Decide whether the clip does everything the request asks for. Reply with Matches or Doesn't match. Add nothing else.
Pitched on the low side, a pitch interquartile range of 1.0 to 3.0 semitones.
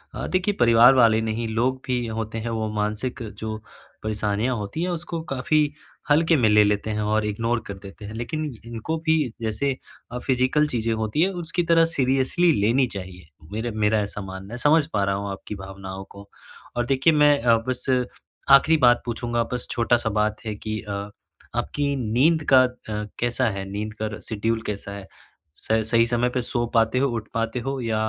Doesn't match